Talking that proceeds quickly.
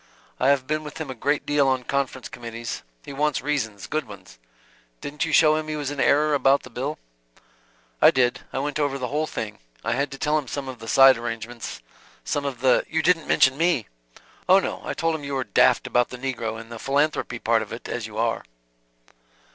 Yes: fast, 225 wpm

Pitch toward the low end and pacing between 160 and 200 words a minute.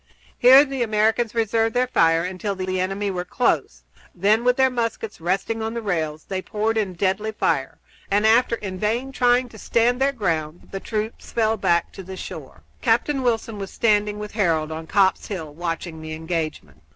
No: high, 210 Hz; average, 190 wpm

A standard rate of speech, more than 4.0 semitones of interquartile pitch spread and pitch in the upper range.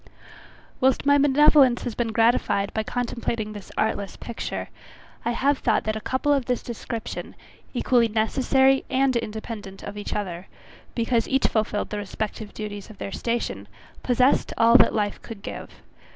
No: average, 155 wpm; average, 3.3 semitones; high, 230 Hz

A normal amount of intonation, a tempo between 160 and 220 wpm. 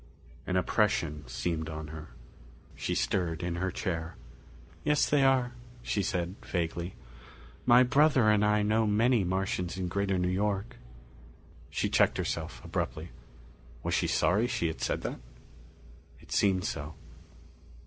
No: average, 4.1 semitones; average, 140 wpm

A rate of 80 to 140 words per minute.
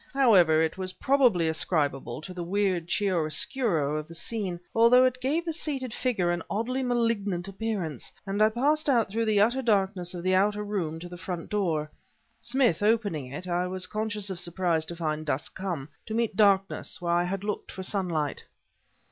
No: average, 185 wpm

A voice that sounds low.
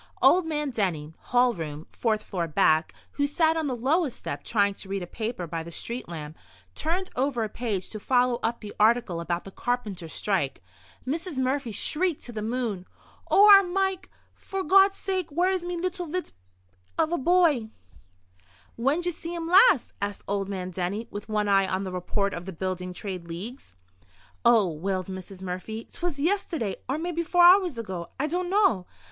No: high, 235 Hz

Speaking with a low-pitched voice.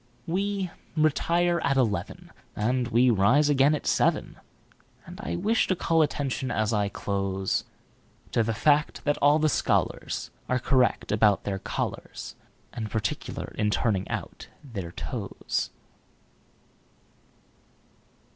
Yes: low, 125 Hz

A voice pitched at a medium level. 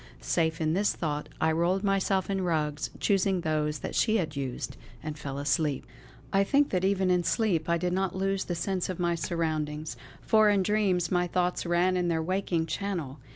Yes: medium, 175 Hz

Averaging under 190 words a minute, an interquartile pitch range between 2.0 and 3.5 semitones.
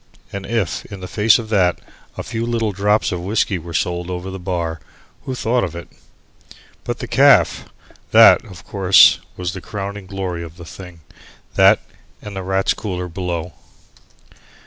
Yes: average, 170 wpm; average, 2.7 semitones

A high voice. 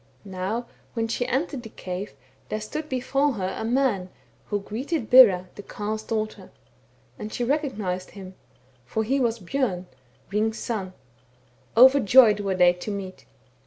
Yes: high, 215 Hz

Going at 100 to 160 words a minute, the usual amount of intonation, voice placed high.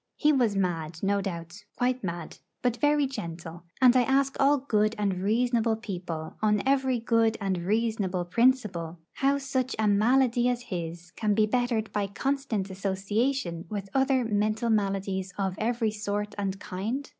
Yes: average, 155 wpm; average, 4.6 semitones; high, 215 Hz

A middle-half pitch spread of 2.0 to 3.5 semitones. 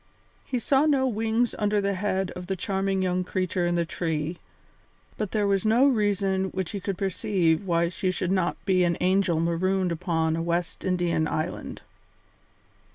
Yes: average, 2.7 semitones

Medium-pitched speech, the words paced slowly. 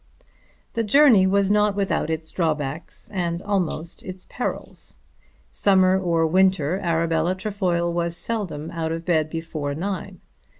Yes: medium, 175 Hz; slow, 130 wpm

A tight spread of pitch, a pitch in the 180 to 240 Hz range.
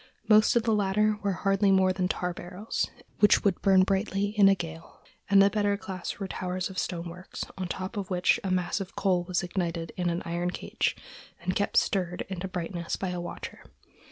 Yes: narrow, 1.9 semitones; medium, 185 Hz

